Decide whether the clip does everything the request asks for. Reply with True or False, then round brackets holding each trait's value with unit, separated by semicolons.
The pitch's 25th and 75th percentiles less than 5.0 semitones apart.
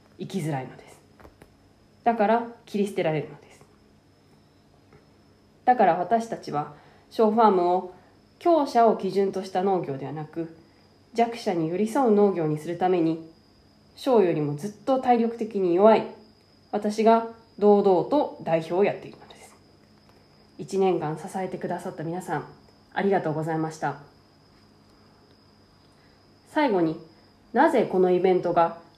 True (4.5 semitones)